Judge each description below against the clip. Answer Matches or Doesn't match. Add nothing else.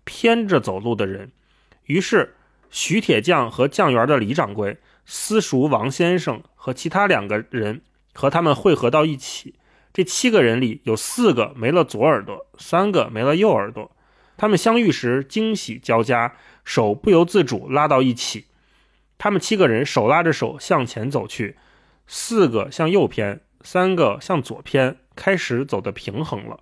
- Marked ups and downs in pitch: Matches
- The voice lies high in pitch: Doesn't match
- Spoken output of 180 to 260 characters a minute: Matches